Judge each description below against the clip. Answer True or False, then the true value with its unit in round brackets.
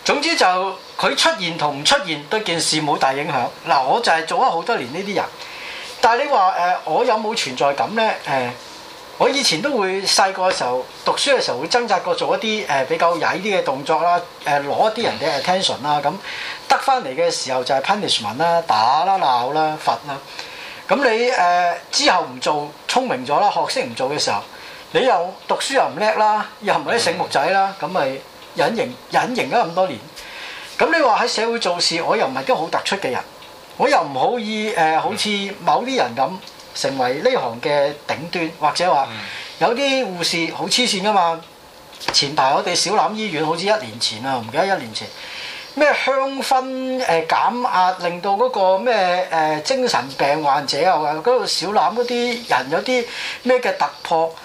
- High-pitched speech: True (195 Hz)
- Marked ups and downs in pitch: True (7.8 semitones)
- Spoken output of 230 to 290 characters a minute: False (305 characters per minute)